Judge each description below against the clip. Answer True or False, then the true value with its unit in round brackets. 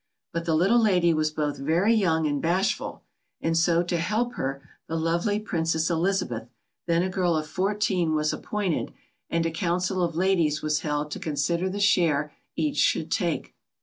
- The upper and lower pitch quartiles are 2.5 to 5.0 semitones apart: True (3.3 semitones)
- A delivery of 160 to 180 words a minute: True (175 wpm)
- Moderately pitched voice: True (170 Hz)